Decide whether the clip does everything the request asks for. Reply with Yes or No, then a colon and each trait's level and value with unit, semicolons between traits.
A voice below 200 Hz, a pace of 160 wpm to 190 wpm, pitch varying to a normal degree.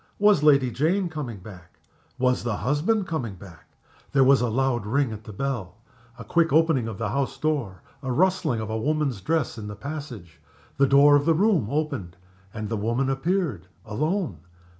No: low, 135 Hz; average, 180 wpm; wide, 5.9 semitones